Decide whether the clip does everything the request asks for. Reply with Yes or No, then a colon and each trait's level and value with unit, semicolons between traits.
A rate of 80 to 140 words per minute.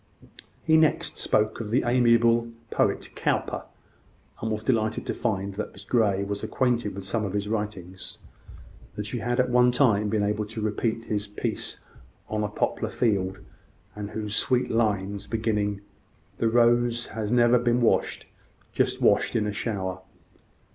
No: average, 155 wpm